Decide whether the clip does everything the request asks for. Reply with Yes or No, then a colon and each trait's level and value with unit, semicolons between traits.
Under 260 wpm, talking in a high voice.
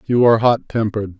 No: average, 200 wpm; low, 110 Hz